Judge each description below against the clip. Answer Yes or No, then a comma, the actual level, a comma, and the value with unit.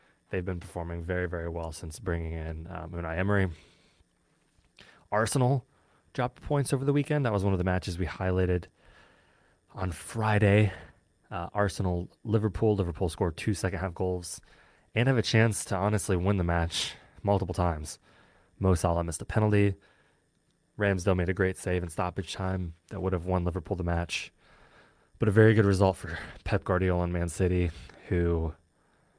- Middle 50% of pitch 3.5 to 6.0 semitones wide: No, average, 3.0 semitones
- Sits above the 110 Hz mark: No, very low, 95 Hz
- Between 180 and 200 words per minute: No, average, 160 wpm